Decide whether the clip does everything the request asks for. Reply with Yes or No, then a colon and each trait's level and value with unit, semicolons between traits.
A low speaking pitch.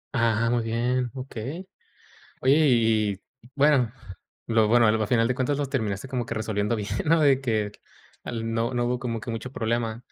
Yes: low, 120 Hz